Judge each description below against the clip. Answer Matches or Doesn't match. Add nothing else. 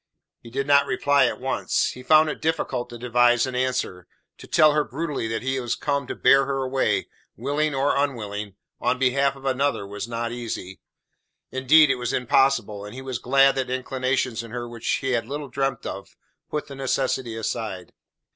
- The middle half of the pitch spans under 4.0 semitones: Matches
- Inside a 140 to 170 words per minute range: Doesn't match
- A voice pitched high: Doesn't match